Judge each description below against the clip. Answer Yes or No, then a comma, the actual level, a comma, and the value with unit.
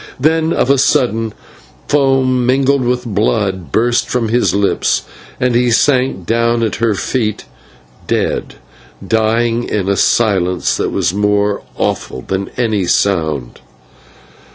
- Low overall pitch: Yes, low, 115 Hz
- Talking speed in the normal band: No, slow, 130 wpm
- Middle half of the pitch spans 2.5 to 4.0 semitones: Yes, average, 3.7 semitones